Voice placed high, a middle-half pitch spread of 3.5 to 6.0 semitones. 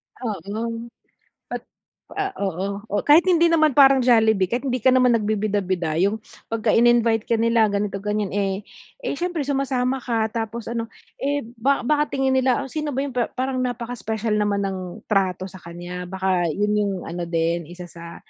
Yes: high, 225 Hz; average, 4.7 semitones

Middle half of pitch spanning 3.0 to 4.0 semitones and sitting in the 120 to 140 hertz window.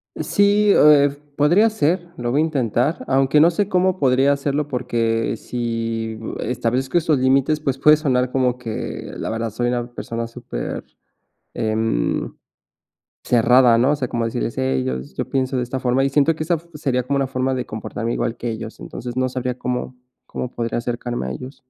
Yes: average, 3.7 semitones; low, 130 Hz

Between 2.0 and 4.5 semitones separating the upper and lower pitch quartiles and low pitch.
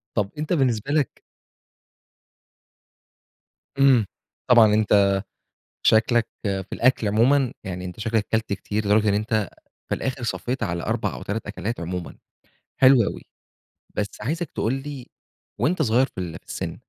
Yes: average, 4.2 semitones; low, 110 Hz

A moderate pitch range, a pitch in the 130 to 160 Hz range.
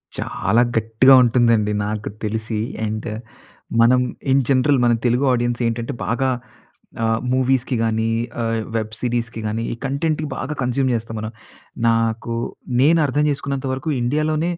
No: average, 3.0 semitones; low, 120 Hz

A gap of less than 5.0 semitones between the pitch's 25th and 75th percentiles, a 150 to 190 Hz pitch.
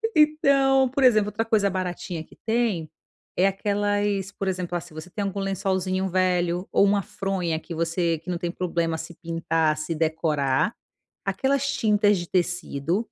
Yes: average, 3.5 semitones; medium, 185 Hz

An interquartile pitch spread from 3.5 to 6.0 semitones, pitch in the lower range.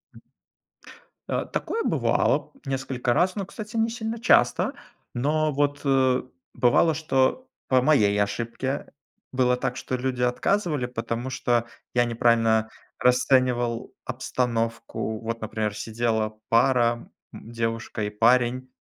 No: average, 2.7 semitones; low, 125 Hz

